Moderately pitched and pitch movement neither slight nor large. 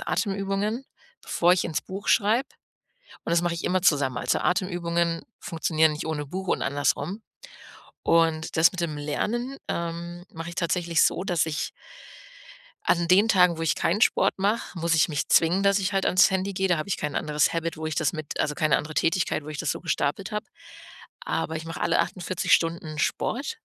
Yes: medium, 170 Hz; average, 3.2 semitones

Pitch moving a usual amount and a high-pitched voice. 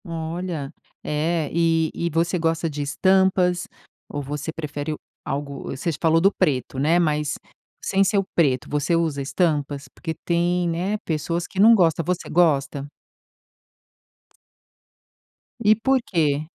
No: average, 3.2 semitones; medium, 165 Hz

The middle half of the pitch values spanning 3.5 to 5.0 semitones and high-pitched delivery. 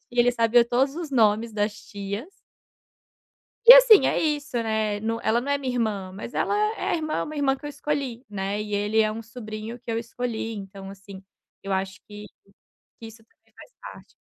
Yes: average, 4.2 semitones; high, 225 Hz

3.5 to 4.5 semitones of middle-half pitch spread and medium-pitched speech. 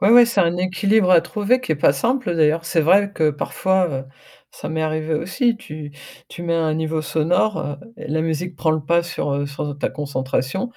Yes: average, 3.8 semitones; medium, 165 Hz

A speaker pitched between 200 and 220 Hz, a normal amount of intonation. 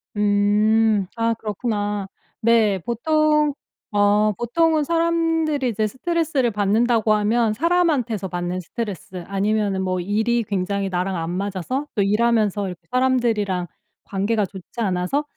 Yes: high, 215 Hz; average, 3.7 semitones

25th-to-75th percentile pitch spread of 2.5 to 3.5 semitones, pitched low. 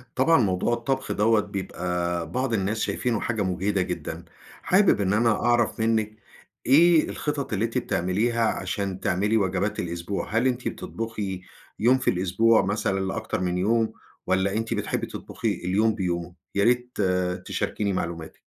No: average, 3.9 semitones; low, 105 Hz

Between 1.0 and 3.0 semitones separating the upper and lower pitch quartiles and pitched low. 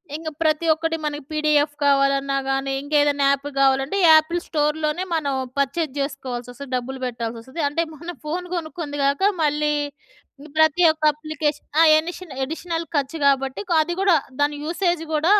No: average, 2.7 semitones; very high, 300 Hz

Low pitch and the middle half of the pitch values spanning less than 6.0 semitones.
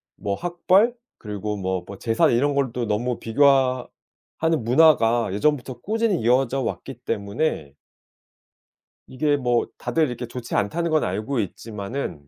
Yes: low, 125 Hz; average, 5.3 semitones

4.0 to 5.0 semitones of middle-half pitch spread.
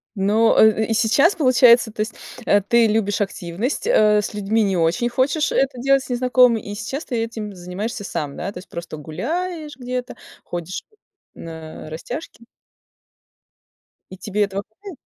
Yes: average, 4.4 semitones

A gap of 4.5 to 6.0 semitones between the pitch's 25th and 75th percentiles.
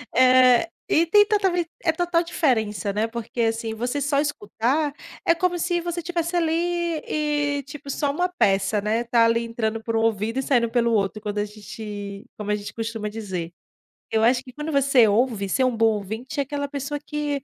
Yes: average, 5.2 semitones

